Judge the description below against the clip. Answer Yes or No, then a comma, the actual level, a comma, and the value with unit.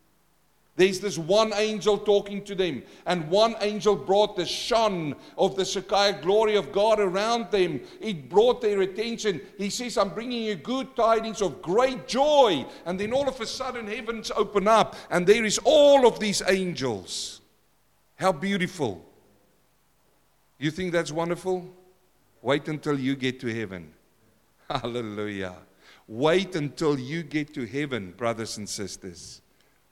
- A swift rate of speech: No, average, 145 wpm